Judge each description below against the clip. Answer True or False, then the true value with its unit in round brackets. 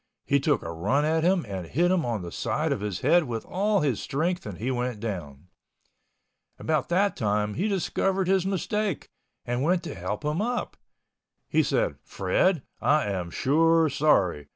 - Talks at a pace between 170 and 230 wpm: True (175 wpm)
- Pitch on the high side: False (145 Hz)